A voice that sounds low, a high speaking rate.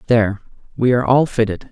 No: low, 115 Hz; average, 175 wpm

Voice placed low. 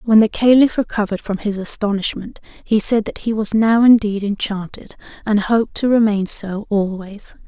No: high, 210 Hz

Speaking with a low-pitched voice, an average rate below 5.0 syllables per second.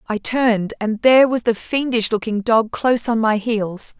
No: high, 225 Hz; 4.8 syllables/s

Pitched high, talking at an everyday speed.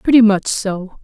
Yes: high, 205 Hz; average, 175 wpm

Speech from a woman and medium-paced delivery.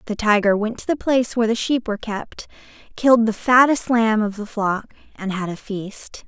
No: female; fast, 210 wpm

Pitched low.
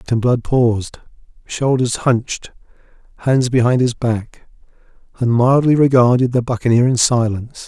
Yes: low, 120 Hz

